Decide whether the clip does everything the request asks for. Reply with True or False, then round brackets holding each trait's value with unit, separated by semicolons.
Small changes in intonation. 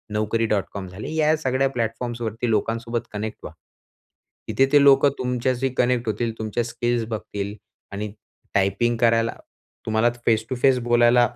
True (2.3 semitones)